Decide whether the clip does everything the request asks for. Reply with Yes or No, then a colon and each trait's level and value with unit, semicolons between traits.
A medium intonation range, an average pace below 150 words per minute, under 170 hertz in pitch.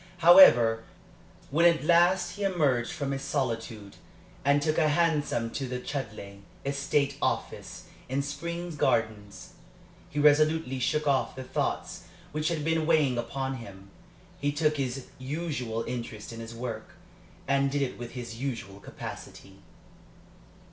Yes: average, 4.5 semitones; average, 140 wpm; low, 135 Hz